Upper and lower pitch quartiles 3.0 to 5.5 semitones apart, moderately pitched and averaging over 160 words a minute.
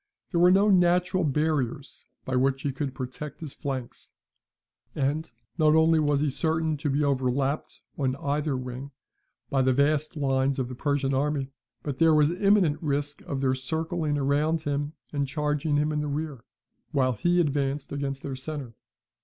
No: narrow, 2.5 semitones; medium, 145 Hz; average, 170 wpm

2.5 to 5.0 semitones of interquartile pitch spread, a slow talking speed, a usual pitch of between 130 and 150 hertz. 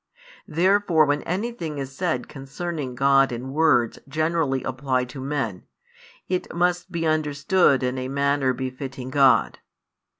Yes: average, 3.7 semitones; slow, 130 wpm; medium, 140 Hz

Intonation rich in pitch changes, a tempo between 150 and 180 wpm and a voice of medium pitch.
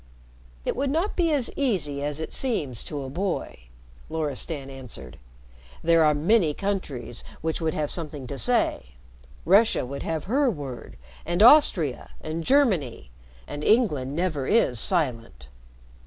No: wide, 6.9 semitones; average, 140 wpm; medium, 160 Hz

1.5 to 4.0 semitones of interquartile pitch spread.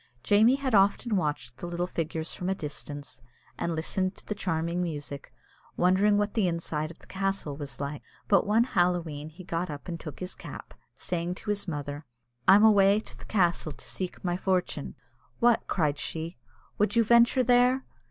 No: average, 4.5 semitones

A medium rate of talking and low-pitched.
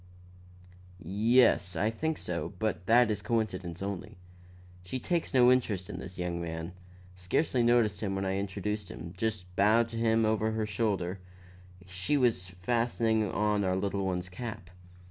Yes: average, 160 wpm; low, 105 Hz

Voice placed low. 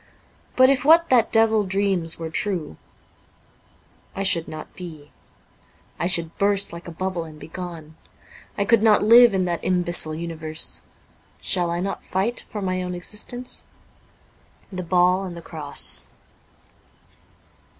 No: medium, 185 Hz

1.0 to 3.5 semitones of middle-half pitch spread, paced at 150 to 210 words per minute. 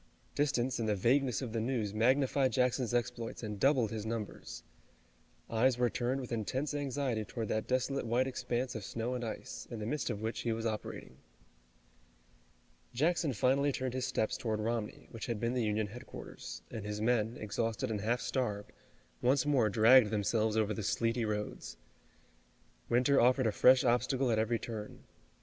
Yes: average, 2.8 semitones; average, 170 wpm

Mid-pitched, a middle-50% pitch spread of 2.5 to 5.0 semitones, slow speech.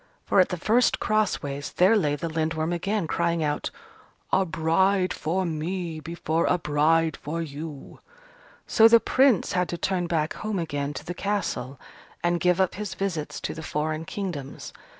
No: medium, 170 Hz; average, 3.3 semitones; average, 170 wpm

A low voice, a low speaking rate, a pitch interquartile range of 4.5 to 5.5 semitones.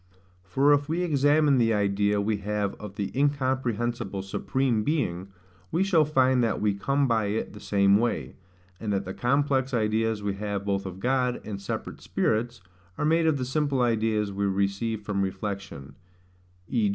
No: low, 110 Hz; average, 170 wpm; average, 4.8 semitones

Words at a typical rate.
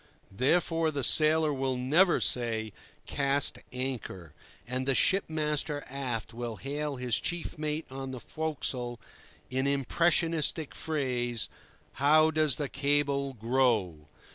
No: slow, 120 wpm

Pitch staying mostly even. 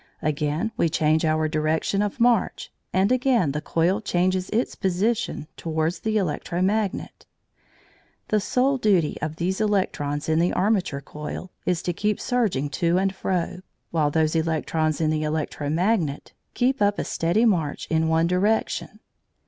No: average, 4.8 semitones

